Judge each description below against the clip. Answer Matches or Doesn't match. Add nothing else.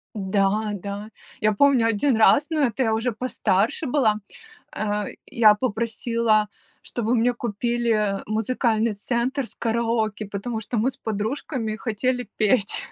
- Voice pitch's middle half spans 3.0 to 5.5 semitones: Doesn't match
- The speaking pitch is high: Matches